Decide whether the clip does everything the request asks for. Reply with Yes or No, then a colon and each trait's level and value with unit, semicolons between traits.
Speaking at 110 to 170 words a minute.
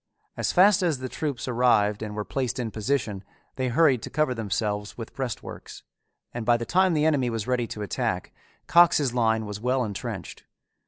No: average, 180 wpm